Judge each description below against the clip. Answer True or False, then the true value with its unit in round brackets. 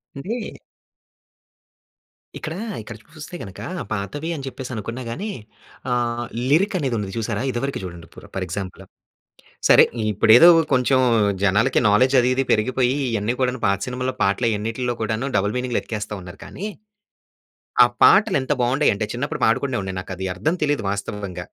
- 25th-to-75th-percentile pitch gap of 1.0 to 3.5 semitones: False (4.4 semitones)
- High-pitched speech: False (120 Hz)